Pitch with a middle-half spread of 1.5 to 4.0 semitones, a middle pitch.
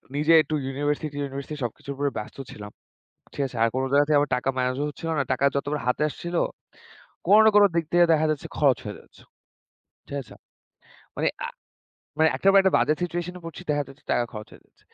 Yes: average, 2.9 semitones; medium, 145 Hz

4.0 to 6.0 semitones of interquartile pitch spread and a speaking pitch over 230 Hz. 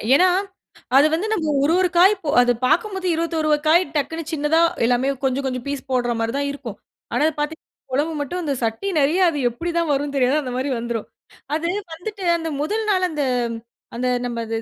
Yes: average, 4.5 semitones; very high, 295 Hz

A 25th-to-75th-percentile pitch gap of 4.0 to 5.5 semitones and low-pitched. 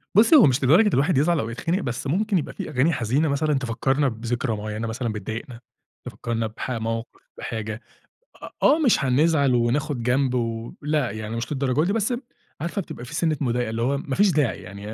Yes: average, 5.0 semitones; low, 130 Hz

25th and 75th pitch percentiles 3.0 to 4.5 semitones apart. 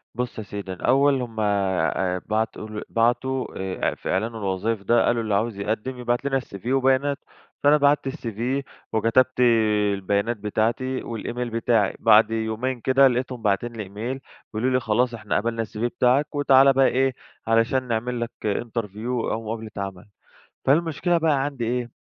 Yes: average, 3.4 semitones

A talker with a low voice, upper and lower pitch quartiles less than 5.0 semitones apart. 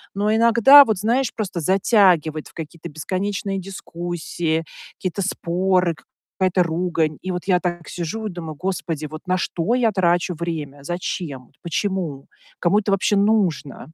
No: medium, 180 Hz; average, 3.3 semitones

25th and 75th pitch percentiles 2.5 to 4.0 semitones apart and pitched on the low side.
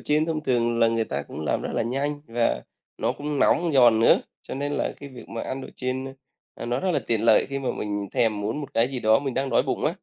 Yes: average, 3.6 semitones; low, 125 Hz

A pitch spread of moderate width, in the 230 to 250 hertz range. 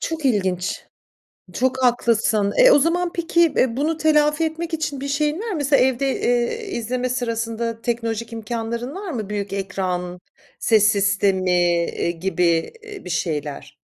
No: wide, 7.1 semitones; high, 235 Hz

